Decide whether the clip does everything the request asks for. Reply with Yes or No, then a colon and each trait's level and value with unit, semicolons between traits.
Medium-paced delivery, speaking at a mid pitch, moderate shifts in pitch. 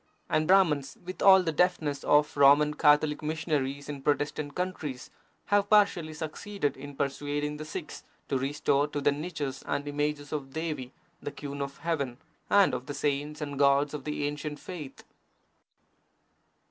No: average, 155 wpm; medium, 145 Hz; narrow, 1.8 semitones